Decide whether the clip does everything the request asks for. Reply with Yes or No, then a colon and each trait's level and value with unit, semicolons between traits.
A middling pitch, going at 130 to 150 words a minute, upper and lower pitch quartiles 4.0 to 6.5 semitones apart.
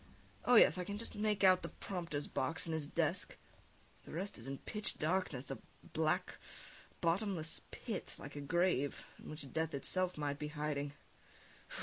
No: medium, 160 Hz; average, 165 wpm; average, 4.5 semitones